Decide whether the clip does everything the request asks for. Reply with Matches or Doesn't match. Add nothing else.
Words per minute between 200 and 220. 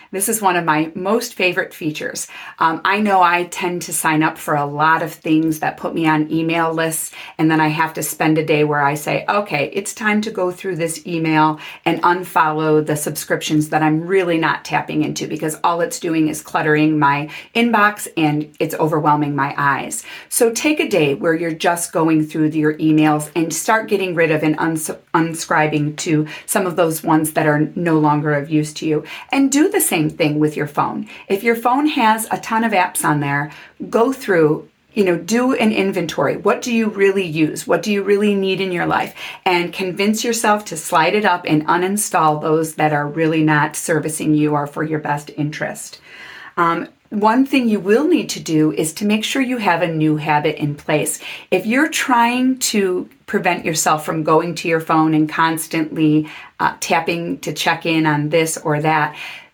Matches